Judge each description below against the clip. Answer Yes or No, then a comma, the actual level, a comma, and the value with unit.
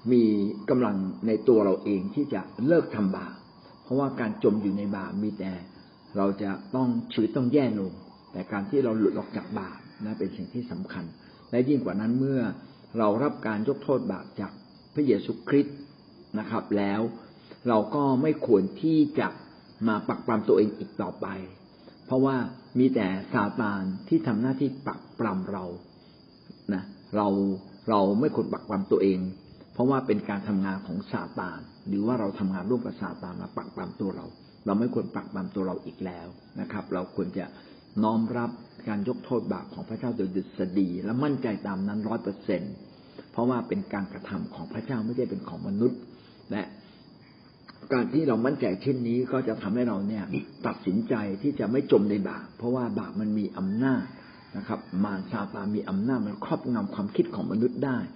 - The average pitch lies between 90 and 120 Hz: Yes, low, 105 Hz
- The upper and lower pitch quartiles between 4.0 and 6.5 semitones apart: Yes, average, 4.5 semitones